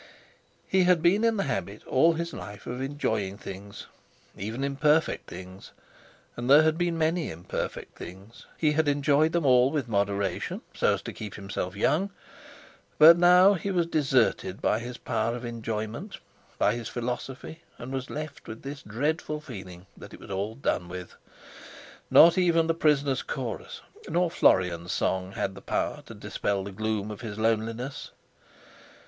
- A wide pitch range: Yes, wide, 7.6 semitones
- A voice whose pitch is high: No, low, 125 Hz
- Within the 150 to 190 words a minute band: Yes, average, 155 wpm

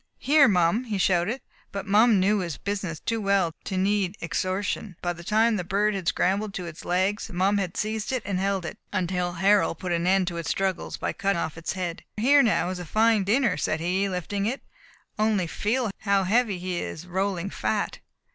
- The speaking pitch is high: Yes, high, 195 Hz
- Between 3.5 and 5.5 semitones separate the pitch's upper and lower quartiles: No, average, 2.9 semitones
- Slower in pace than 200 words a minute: No, fast, 205 wpm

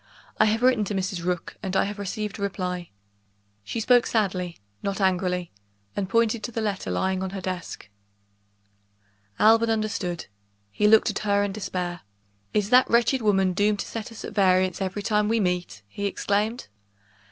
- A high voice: Yes, high, 200 Hz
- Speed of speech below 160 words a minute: No, average, 175 wpm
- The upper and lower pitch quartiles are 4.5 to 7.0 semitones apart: No, average, 2.8 semitones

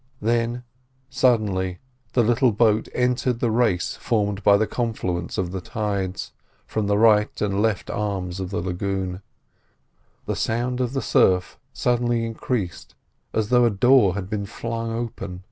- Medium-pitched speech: No, low, 105 Hz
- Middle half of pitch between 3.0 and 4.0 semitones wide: Yes, average, 3.5 semitones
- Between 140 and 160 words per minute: Yes, average, 150 wpm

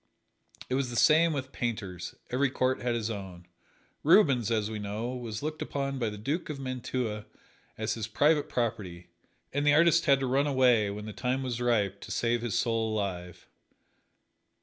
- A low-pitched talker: Yes, low, 120 Hz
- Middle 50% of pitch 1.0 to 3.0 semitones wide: No, average, 4.2 semitones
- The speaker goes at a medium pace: Yes, average, 180 wpm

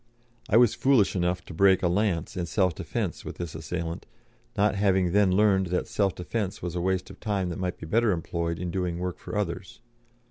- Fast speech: Yes, fast, 210 wpm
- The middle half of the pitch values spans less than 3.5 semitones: Yes, narrow, 2.5 semitones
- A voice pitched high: No, very low, 90 Hz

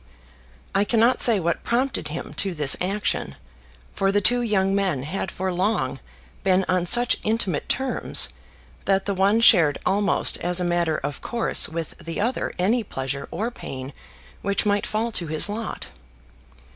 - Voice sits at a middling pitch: No, high, 195 Hz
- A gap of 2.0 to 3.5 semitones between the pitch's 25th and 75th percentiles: No, average, 4.2 semitones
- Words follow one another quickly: No, average, 160 wpm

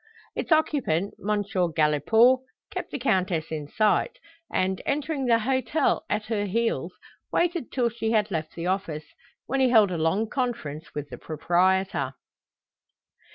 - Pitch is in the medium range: No, high, 205 Hz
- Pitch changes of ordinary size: No, wide, 6.6 semitones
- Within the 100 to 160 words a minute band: Yes, average, 145 wpm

